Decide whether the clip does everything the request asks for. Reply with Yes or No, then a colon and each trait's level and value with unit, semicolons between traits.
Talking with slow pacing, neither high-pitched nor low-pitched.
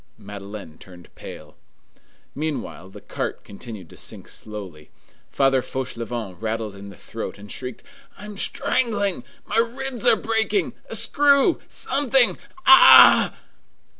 No: slow, 125 wpm; low, 130 Hz